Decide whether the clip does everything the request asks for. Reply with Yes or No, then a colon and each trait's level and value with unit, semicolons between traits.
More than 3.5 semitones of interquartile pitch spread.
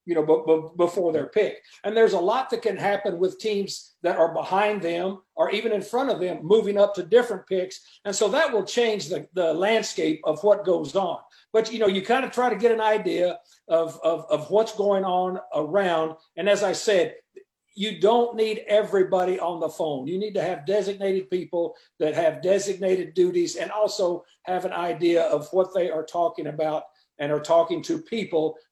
Yes: average, 4.1 semitones